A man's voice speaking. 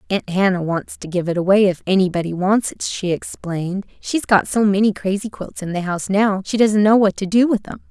No: female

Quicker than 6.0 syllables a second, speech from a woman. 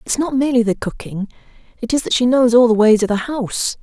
Yes: 6.3 syllables/s; female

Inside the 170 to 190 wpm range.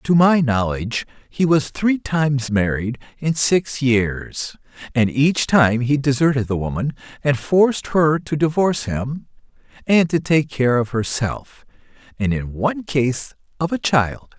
No: average, 155 wpm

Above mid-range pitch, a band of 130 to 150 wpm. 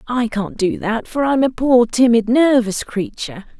No: high, 230 Hz; average, 200 wpm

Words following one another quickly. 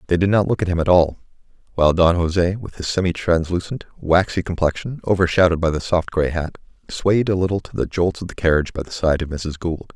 Yes: fast, 230 wpm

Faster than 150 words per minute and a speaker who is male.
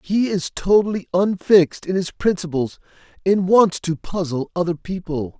No: average, 145 wpm; male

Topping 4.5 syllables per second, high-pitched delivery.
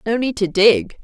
No: 4.4 syllables/s; high, 215 Hz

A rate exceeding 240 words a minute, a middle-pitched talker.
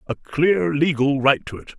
No: average, 200 wpm; medium, 150 Hz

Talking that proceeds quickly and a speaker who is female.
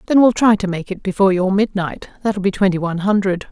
Yes: fast, 220 wpm; female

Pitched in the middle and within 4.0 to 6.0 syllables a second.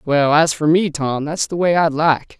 Yes: medium, 155 Hz; 4.4 syllables/s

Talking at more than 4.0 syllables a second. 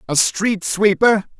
No: 3.5 syllables/s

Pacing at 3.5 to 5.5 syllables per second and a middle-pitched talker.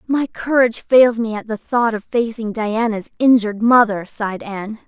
No: 5.0 syllables/s; high, 225 Hz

